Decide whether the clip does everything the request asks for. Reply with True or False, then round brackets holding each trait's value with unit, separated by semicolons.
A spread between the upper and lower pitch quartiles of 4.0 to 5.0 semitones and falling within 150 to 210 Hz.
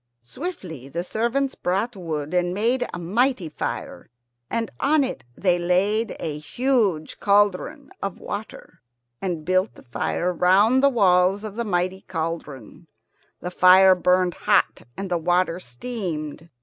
True (4.4 semitones; 185 Hz)